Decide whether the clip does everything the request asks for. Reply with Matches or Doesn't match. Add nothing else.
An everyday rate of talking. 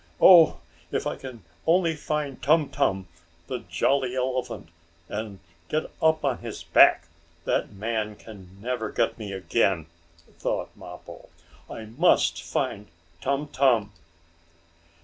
Doesn't match